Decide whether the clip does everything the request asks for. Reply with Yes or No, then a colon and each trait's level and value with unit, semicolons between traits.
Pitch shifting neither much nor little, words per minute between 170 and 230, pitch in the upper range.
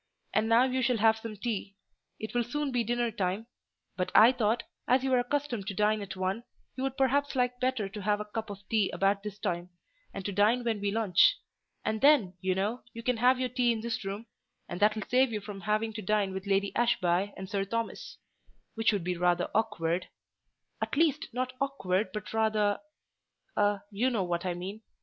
Yes: average, 3.7 semitones; average, 200 wpm; high, 215 Hz